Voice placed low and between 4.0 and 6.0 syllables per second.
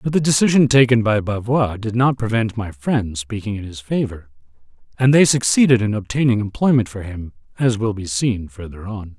Yes: low, 110 Hz; 5.2 syllables/s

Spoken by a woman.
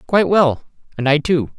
No: male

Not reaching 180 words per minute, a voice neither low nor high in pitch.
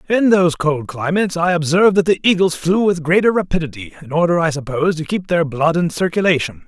No: fast, 205 wpm; medium, 170 Hz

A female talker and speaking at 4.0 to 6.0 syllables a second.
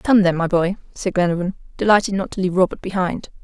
No: female; 6.5 syllables/s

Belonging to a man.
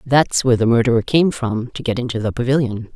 No: female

